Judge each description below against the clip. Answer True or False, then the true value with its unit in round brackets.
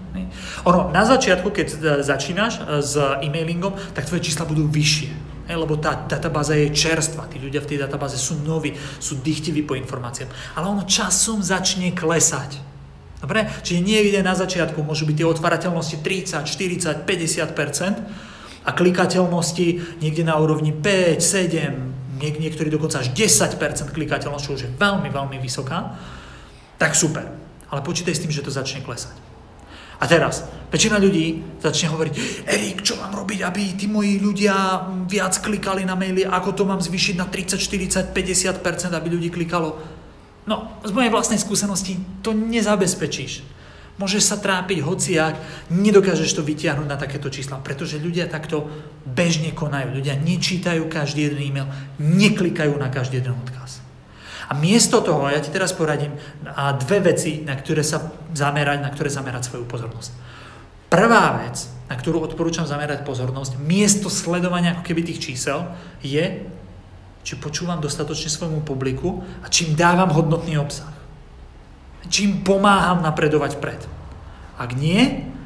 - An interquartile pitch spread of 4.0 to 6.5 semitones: True (4.3 semitones)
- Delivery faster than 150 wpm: False (145 wpm)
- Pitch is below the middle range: False (160 Hz)